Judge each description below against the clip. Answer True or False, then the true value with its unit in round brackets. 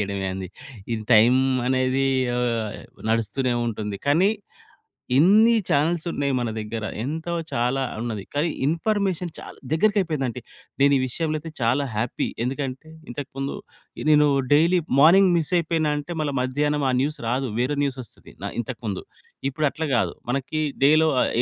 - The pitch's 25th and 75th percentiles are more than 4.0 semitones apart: True (4.7 semitones)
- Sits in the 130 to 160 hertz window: True (140 Hz)